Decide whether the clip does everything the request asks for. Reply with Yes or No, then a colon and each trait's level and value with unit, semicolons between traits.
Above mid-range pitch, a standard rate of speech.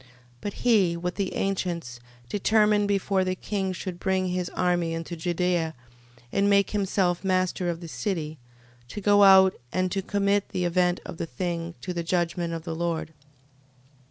No: medium, 180 Hz; average, 170 wpm